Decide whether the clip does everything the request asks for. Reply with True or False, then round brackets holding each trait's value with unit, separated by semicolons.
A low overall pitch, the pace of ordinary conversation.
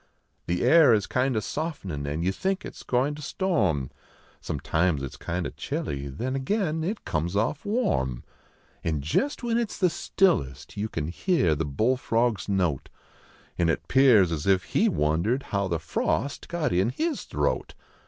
True (105 Hz; 185 wpm)